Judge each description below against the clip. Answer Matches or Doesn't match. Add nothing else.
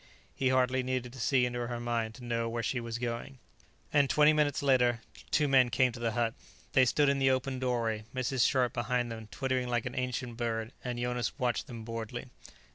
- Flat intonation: Matches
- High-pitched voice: Doesn't match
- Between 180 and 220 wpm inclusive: Matches